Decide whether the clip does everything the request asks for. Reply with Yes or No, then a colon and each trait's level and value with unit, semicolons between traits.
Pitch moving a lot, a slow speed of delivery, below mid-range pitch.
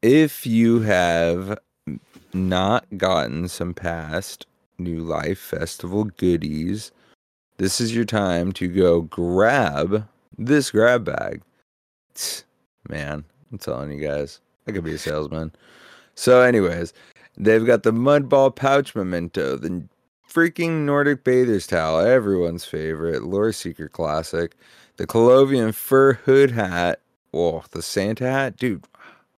Yes: wide, 6.6 semitones; slow, 120 wpm; very low, 95 Hz